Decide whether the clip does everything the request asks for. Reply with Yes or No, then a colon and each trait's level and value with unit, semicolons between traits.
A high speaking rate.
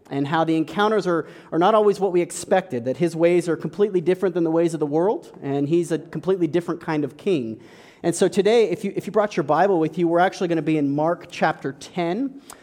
Yes: fast, 245 wpm